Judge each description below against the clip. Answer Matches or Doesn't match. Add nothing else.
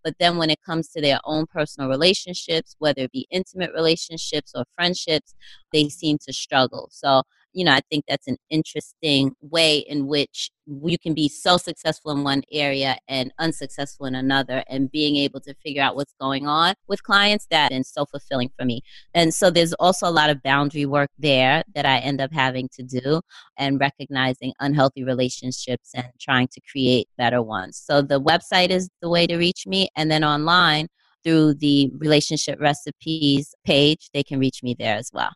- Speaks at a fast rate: Doesn't match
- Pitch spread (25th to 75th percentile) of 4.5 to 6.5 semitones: Doesn't match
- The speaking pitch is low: Doesn't match